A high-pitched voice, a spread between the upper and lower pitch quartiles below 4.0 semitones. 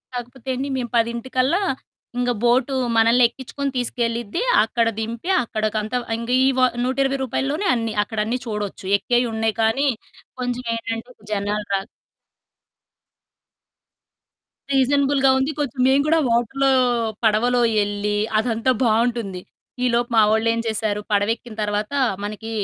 Yes: high, 235 Hz; average, 2.8 semitones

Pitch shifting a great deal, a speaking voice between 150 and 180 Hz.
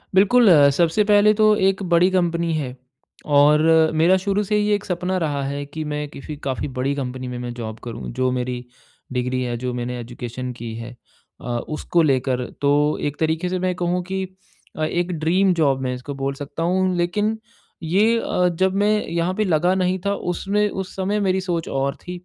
Yes: wide, 6.0 semitones; medium, 165 Hz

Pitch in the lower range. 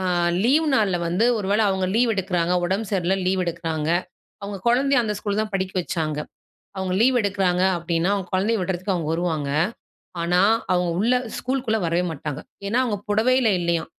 No: high, 190 Hz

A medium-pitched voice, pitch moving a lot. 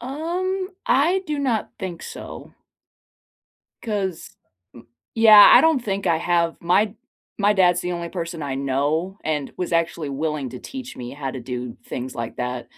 Yes: medium, 175 Hz; wide, 7.6 semitones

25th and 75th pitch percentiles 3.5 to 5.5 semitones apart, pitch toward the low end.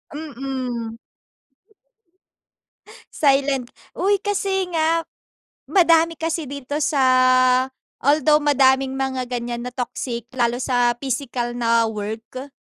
No: average, 4.1 semitones; very high, 265 Hz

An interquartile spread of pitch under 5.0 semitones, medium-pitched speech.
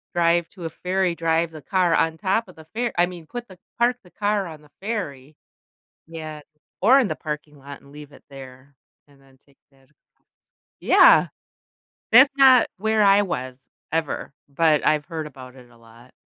No: wide, 5.4 semitones; medium, 165 Hz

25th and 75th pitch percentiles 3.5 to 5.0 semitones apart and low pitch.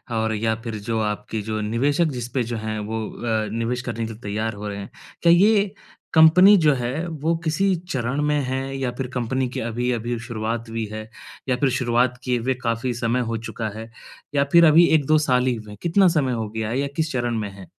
Yes: average, 3.9 semitones; low, 120 Hz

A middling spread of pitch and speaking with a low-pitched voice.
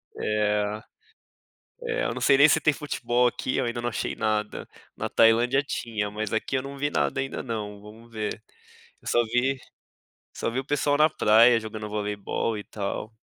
Yes: average, 3.7 semitones; low, 115 Hz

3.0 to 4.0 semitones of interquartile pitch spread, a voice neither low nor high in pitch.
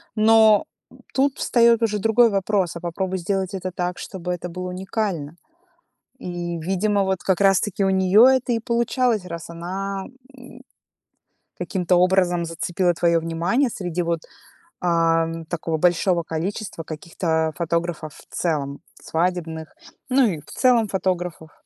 Yes: average, 3.4 semitones; medium, 180 Hz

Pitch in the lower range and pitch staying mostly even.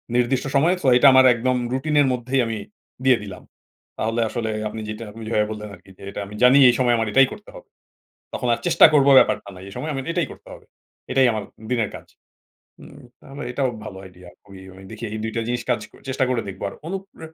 No: low, 125 Hz; average, 3.6 semitones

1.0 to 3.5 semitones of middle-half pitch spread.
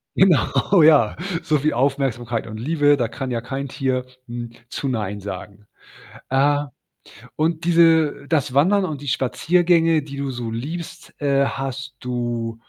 No: average, 4.4 semitones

